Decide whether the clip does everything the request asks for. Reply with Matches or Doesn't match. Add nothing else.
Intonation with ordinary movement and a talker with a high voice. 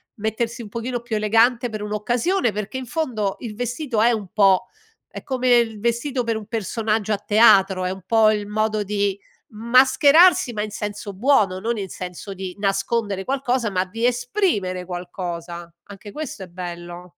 Matches